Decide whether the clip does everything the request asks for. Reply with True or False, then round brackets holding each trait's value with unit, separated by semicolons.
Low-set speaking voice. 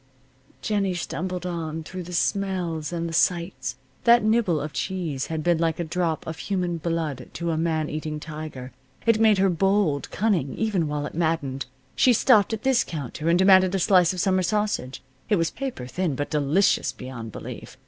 False (170 Hz)